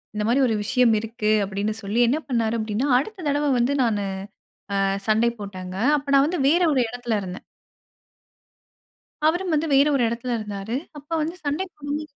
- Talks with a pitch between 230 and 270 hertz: Yes, high, 240 Hz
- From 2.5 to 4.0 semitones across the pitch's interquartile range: No, average, 5.2 semitones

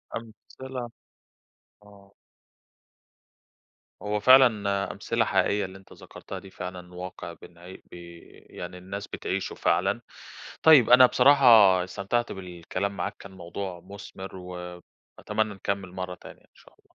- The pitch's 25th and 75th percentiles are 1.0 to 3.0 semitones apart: Yes, narrow, 2.6 semitones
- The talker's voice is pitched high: No, very low, 95 Hz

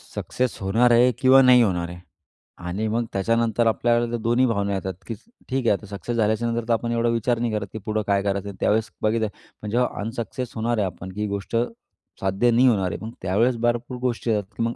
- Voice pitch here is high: No, low, 115 Hz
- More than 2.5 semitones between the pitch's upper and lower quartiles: Yes, average, 2.9 semitones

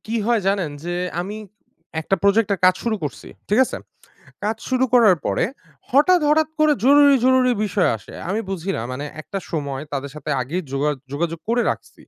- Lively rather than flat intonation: Yes, wide, 7.6 semitones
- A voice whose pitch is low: No, high, 200 Hz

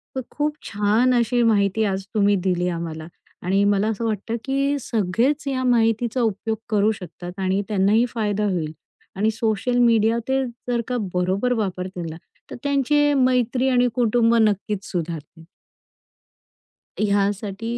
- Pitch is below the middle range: No, high, 215 Hz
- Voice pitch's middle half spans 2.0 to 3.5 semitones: No, average, 4.0 semitones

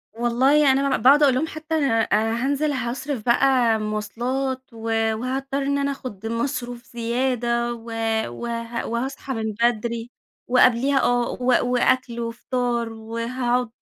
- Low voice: No, high, 245 Hz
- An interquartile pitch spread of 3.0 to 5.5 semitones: No, narrow, 2.4 semitones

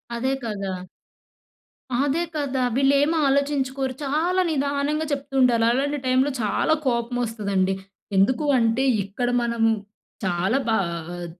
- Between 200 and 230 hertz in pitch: No, very high, 260 Hz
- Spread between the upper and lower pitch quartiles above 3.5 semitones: Yes, average, 3.9 semitones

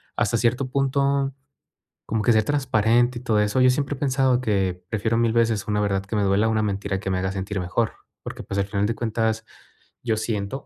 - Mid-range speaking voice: No, low, 110 Hz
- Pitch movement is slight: No, average, 3.8 semitones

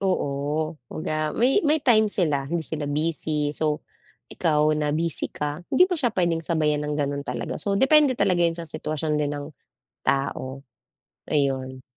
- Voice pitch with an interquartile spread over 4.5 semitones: No, average, 2.9 semitones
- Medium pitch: Yes, medium, 155 Hz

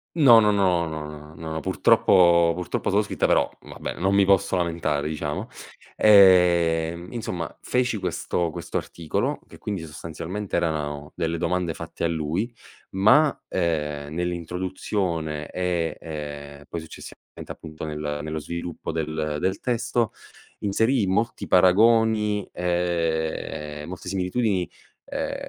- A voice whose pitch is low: Yes, very low, 85 Hz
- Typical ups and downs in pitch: Yes, average, 3.6 semitones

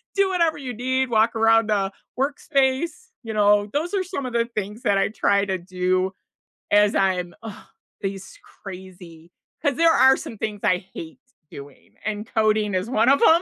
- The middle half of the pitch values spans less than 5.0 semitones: No, wide, 5.4 semitones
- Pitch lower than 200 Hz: No, high, 215 Hz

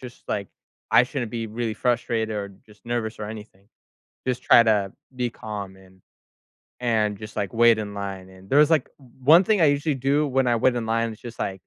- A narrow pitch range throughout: No, average, 3.2 semitones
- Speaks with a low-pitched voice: Yes, low, 115 Hz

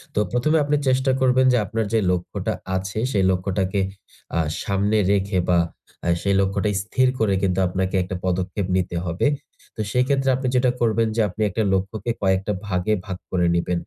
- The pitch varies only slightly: No, average, 3.6 semitones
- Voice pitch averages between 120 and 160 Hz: No, low, 100 Hz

